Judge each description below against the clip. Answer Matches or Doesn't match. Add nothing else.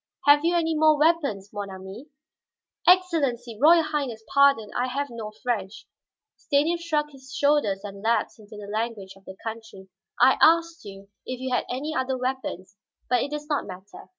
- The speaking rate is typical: Matches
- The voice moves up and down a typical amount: Doesn't match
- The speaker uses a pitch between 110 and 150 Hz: Doesn't match